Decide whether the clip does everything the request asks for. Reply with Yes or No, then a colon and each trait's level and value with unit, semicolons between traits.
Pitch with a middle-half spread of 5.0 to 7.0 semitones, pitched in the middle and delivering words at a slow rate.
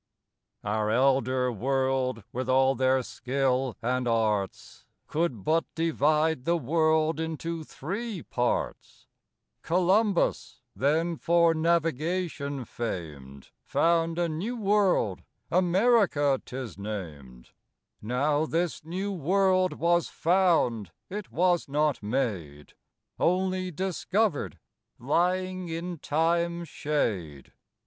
Yes: wide, 5.4 semitones; medium, 155 Hz; slow, 95 wpm